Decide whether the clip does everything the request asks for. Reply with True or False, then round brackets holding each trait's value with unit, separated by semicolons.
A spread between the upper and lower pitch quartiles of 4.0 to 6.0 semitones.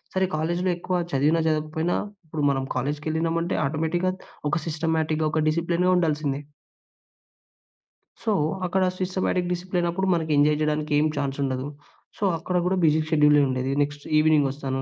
False (2.8 semitones)